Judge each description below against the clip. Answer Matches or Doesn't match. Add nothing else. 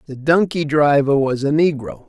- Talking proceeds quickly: Doesn't match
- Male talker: Matches